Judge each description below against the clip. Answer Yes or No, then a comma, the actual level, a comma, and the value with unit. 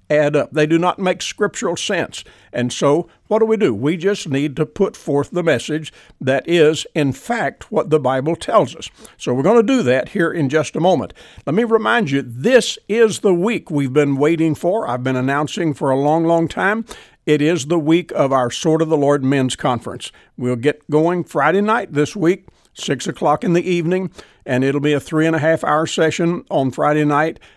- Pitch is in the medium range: Yes, medium, 155 Hz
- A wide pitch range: No, average, 3.6 semitones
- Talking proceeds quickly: Yes, fast, 215 wpm